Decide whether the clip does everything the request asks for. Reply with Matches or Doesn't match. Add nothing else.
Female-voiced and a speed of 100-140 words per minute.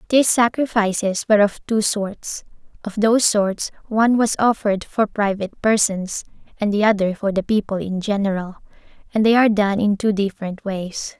Doesn't match